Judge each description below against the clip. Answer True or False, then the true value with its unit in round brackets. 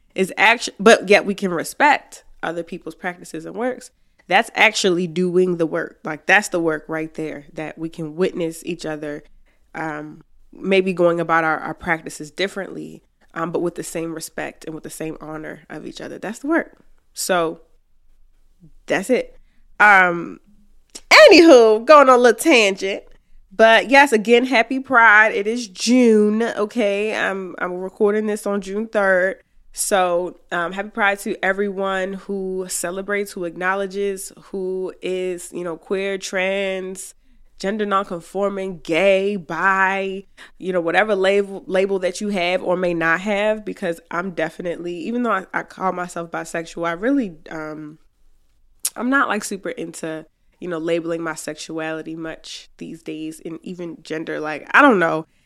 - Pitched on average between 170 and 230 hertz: True (185 Hz)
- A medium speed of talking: True (155 wpm)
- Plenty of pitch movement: False (3.6 semitones)